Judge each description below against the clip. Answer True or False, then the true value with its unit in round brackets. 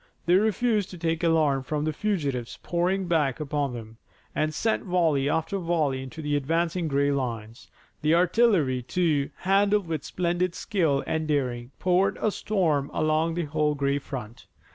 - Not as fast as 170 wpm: True (160 wpm)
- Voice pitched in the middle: True (155 Hz)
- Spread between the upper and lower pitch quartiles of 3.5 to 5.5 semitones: True (4.3 semitones)